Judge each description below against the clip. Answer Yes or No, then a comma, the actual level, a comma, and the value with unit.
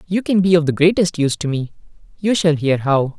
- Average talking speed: No, fast, 225 wpm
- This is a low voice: No, medium, 165 Hz